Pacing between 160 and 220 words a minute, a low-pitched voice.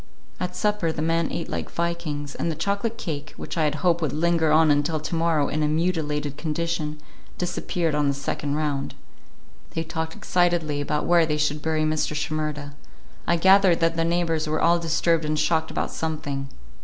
No: average, 185 wpm; medium, 160 Hz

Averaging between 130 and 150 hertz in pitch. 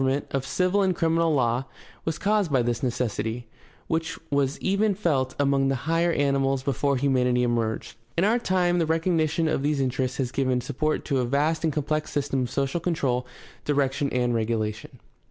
Yes: medium, 140 Hz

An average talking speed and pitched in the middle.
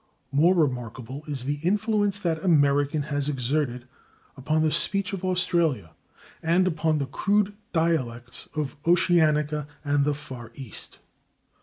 No: slow, 130 wpm; medium, 150 Hz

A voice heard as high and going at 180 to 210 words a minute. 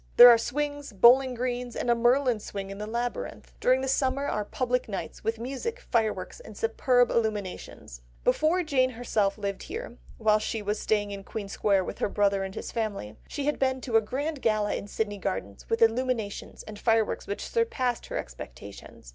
Yes: high, 225 Hz; average, 190 wpm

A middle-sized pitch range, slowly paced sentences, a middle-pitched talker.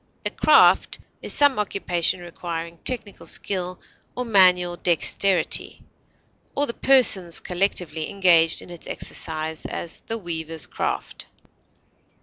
Yes: average, 3.2 semitones; slow, 115 wpm; medium, 180 Hz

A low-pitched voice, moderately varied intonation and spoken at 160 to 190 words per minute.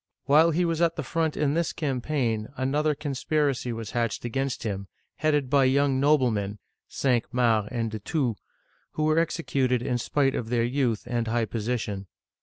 Yes: low, 130 Hz; average, 4.3 semitones; average, 170 wpm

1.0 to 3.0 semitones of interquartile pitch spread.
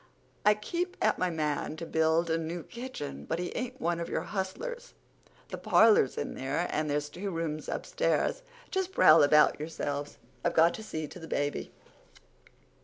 No: wide, 5.4 semitones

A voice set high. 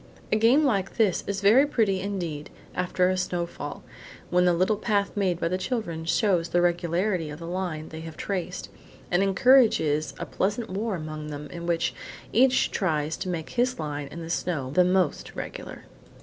No: medium, 180 Hz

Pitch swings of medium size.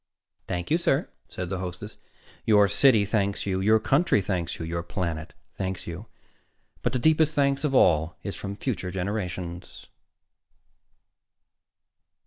Yes: average, 4.2 semitones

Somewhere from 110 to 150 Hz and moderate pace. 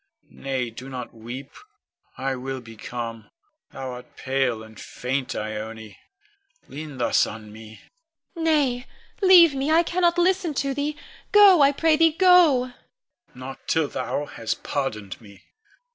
Yes: low, 135 Hz; average, 145 wpm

